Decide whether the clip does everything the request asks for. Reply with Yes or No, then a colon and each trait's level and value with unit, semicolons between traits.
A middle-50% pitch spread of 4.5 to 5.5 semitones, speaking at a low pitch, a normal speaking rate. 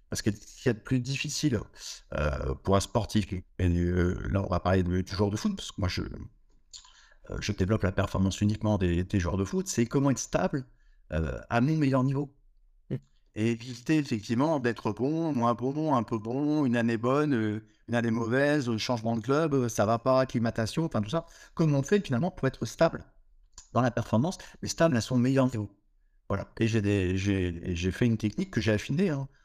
Yes: average, 5.1 semitones; low, 115 Hz; average, 210 wpm